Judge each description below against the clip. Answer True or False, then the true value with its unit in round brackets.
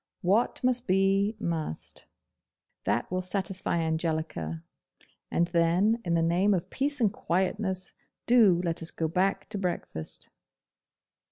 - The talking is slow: True (125 wpm)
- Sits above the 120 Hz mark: True (185 Hz)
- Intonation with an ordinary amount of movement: True (3.3 semitones)